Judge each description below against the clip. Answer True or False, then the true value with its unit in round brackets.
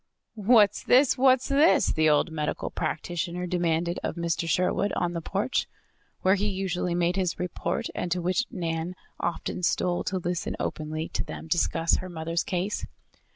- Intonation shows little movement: True (2.3 semitones)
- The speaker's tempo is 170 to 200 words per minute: False (160 wpm)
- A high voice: False (175 Hz)